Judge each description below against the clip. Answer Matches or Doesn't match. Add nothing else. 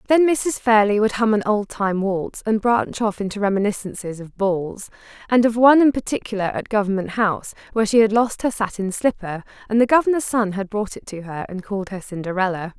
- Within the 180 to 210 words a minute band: Matches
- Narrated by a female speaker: Matches